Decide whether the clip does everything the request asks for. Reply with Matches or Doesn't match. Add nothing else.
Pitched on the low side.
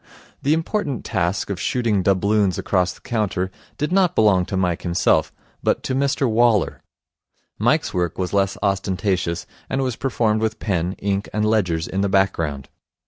Matches